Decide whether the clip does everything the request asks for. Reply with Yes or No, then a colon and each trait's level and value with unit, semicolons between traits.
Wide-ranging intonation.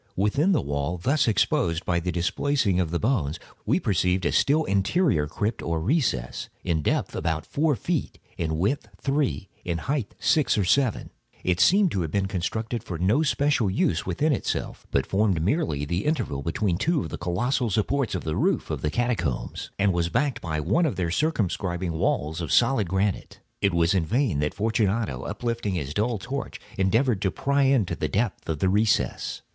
Yes: wide, 7.4 semitones